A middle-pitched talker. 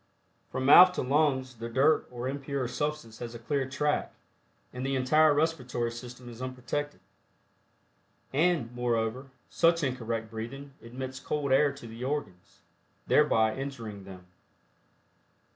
No: low, 130 Hz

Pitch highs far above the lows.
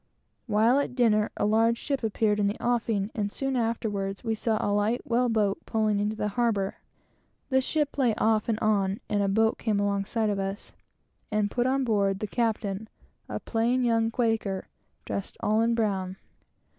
No: narrow, 2.4 semitones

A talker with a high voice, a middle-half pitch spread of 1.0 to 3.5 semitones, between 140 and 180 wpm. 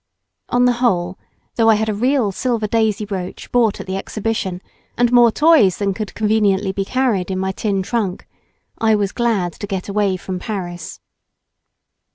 Yes: high, 210 Hz; average, 3.2 semitones; average, 175 wpm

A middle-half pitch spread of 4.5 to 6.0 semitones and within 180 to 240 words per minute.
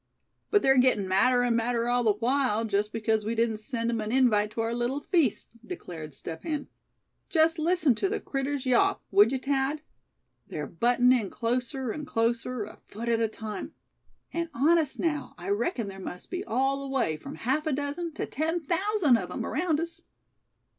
Yes: average, 4.9 semitones; average, 190 wpm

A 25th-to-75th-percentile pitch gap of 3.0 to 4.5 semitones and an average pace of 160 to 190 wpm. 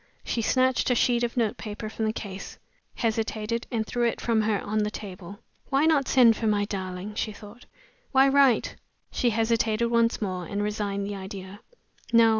No: narrow, 2.5 semitones; average, 180 wpm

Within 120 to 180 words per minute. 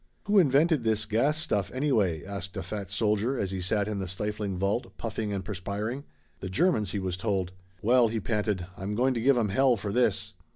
No: fast, 205 wpm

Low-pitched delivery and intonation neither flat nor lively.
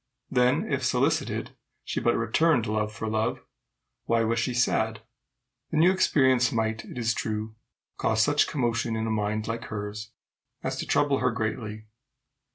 No: low, 115 Hz; narrow, 2.3 semitones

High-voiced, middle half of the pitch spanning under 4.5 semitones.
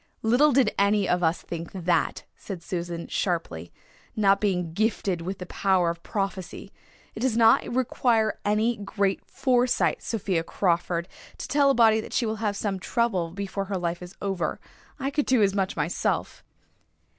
Yes: high, 195 Hz; average, 4.0 semitones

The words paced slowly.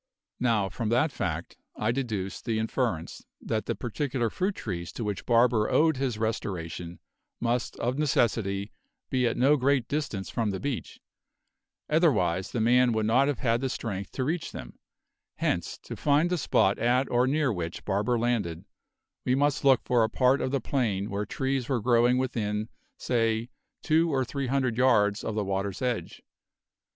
No: average, 170 wpm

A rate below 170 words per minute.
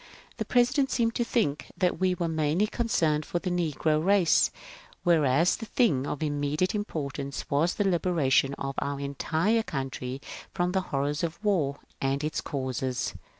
Yes: average, 155 wpm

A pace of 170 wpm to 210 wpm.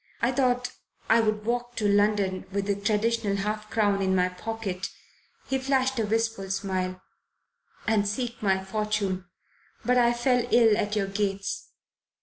No: average, 150 wpm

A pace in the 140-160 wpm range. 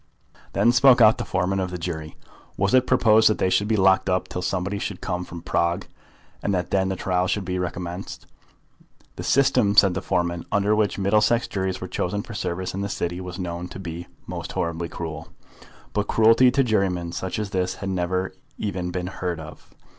No: average, 200 wpm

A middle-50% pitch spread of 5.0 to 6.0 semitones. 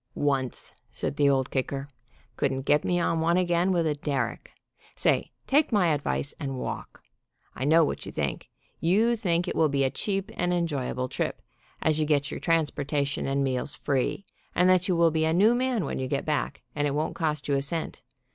No: average, 3.8 semitones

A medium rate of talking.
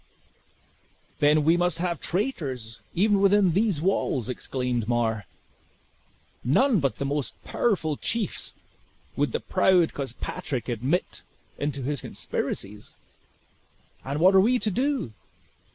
No: slow, 120 wpm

